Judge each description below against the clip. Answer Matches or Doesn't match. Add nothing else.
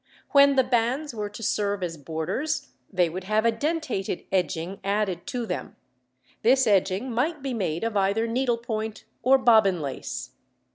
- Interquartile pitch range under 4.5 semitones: Doesn't match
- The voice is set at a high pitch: Matches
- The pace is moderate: Matches